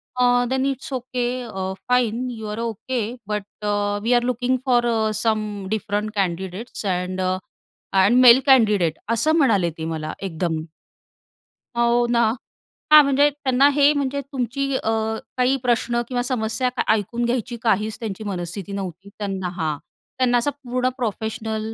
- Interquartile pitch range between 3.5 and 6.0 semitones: Yes, average, 3.8 semitones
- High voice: Yes, high, 235 Hz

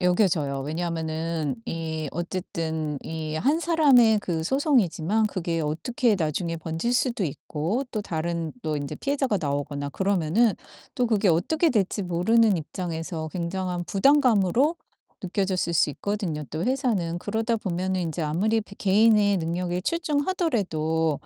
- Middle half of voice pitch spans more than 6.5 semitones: No, wide, 5.5 semitones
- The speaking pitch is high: No, medium, 180 Hz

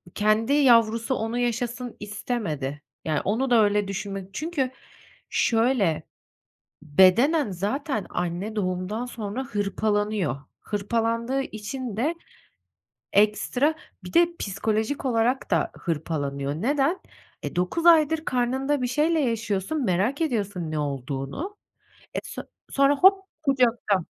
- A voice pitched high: Yes, high, 225 Hz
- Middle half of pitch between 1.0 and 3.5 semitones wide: No, average, 5.3 semitones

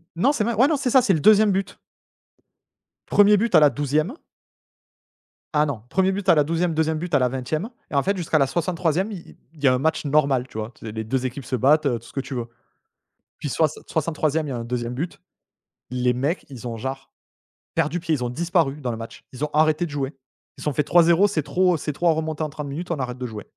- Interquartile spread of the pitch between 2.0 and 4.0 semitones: No, average, 4.7 semitones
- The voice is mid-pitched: Yes, medium, 150 Hz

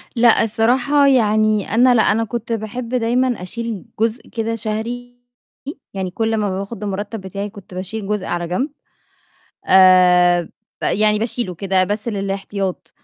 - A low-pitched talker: No, high, 215 Hz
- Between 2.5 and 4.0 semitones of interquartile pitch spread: Yes, average, 3.1 semitones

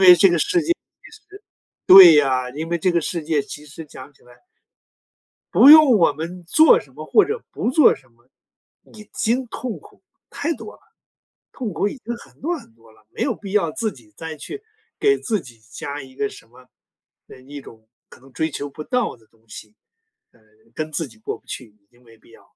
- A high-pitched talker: No, medium, 160 Hz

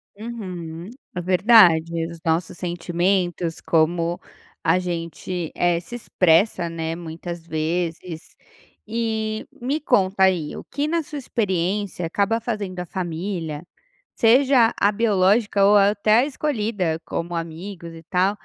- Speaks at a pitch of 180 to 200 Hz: Yes, medium, 185 Hz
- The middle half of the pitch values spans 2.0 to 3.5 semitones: No, average, 4.1 semitones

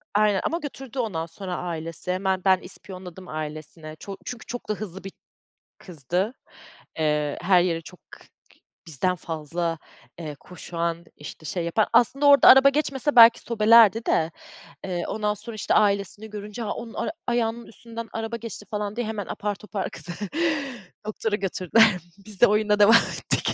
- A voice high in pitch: Yes, high, 200 Hz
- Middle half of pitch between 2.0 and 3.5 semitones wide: No, average, 4.4 semitones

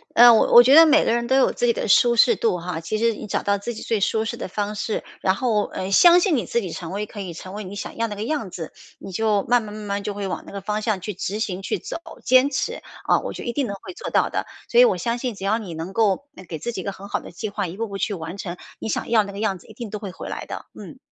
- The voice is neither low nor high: No, high, 210 Hz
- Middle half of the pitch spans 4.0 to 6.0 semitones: No, average, 3.3 semitones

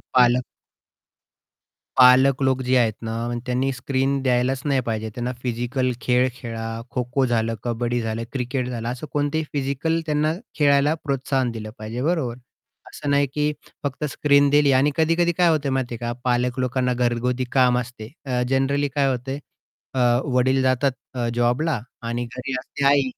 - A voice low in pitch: Yes, low, 130 Hz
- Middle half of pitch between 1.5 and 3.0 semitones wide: Yes, narrow, 2.4 semitones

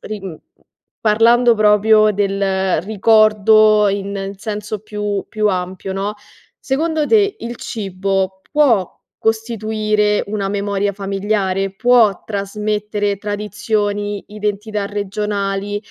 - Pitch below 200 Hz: No, high, 205 Hz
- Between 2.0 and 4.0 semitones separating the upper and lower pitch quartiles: No, narrow, 1.5 semitones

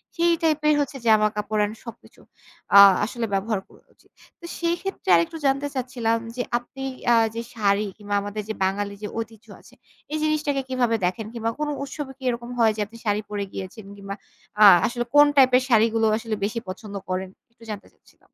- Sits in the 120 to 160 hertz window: No, high, 225 Hz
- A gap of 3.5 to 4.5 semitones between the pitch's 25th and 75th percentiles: Yes, average, 4.0 semitones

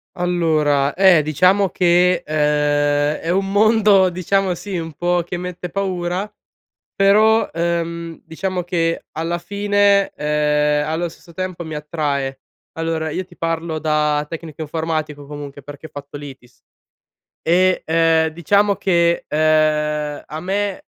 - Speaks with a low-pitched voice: No, medium, 165 Hz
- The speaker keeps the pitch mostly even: No, average, 3.3 semitones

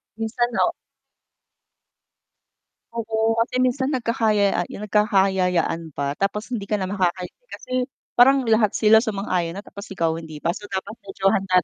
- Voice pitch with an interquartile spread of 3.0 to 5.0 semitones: Yes, average, 3.4 semitones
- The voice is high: Yes, high, 205 Hz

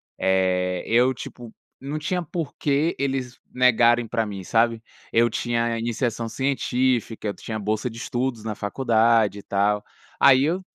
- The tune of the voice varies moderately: Yes, average, 3.2 semitones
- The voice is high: No, low, 120 Hz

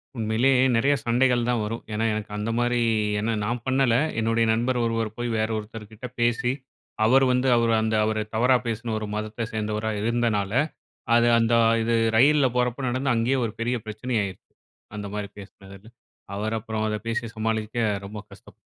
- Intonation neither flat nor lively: No, narrow, 2.0 semitones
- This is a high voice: No, low, 115 Hz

